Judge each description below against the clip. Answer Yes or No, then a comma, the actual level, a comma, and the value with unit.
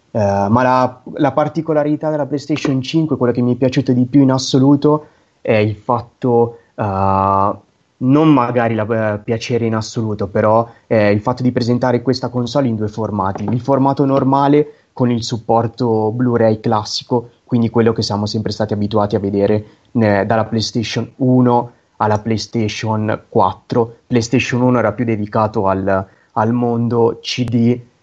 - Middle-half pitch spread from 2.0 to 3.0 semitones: Yes, average, 2.7 semitones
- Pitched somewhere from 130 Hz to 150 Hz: No, low, 120 Hz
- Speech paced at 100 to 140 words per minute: No, average, 155 wpm